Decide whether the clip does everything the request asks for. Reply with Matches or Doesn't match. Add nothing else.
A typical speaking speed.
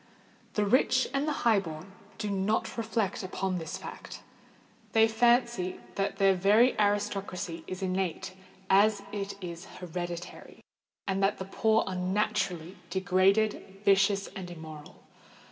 Doesn't match